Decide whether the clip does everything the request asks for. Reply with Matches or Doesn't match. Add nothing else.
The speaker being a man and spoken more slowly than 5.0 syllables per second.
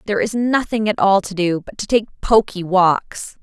Doesn't match